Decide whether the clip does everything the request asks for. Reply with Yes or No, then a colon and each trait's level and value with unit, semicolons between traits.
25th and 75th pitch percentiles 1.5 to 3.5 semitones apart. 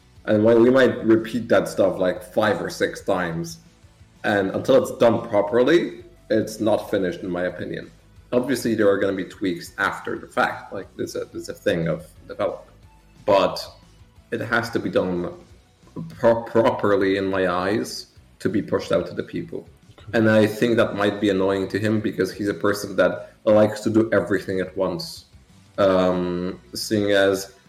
Yes: average, 2.8 semitones